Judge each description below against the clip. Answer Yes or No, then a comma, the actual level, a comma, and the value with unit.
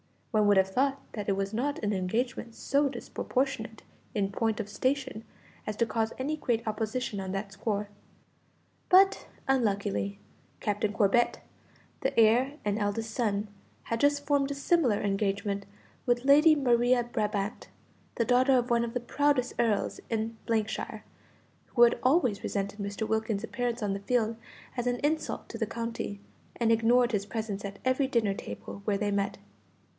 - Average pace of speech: Yes, average, 160 wpm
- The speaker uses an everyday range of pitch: Yes, average, 3.6 semitones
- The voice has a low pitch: No, high, 225 Hz